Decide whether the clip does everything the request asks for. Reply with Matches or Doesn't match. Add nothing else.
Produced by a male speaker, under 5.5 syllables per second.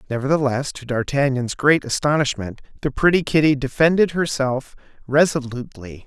Matches